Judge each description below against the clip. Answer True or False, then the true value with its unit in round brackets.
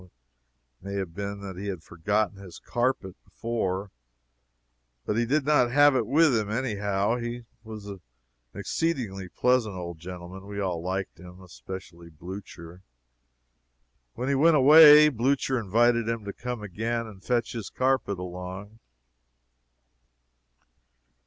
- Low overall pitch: True (105 Hz)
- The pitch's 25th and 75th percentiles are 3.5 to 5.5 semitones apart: True (4.6 semitones)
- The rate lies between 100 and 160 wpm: True (135 wpm)